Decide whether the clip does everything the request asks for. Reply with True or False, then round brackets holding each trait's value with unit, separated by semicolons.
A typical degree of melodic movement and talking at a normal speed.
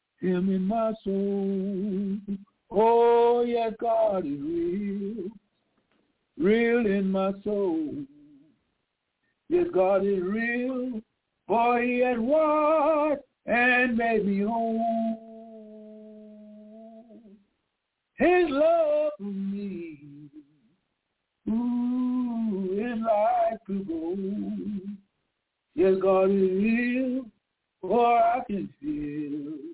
False (4.1 semitones; 85 wpm)